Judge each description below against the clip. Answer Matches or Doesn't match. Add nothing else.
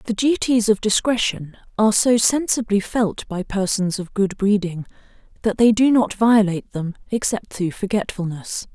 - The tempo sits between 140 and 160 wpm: Matches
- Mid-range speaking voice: Doesn't match